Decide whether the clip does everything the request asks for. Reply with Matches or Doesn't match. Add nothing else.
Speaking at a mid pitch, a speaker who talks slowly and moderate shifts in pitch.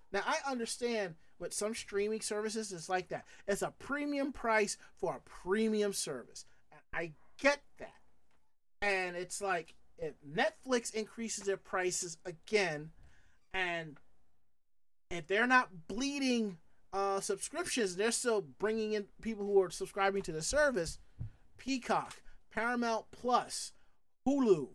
Doesn't match